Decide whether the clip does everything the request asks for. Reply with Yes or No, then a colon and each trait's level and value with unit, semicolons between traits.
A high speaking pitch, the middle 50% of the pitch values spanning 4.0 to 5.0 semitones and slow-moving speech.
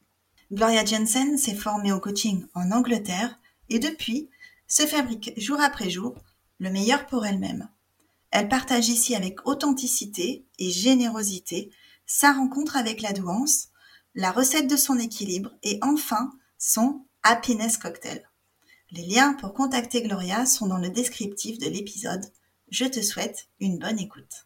Yes: high, 230 Hz; average, 4.6 semitones; slow, 140 wpm